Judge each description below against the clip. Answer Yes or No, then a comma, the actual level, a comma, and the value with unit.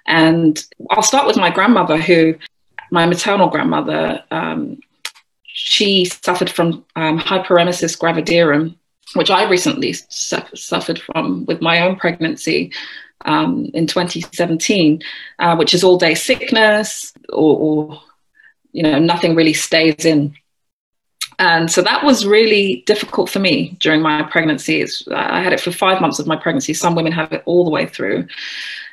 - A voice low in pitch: No, medium, 170 Hz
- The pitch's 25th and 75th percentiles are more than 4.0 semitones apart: No, narrow, 2.5 semitones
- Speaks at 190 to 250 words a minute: No, average, 150 wpm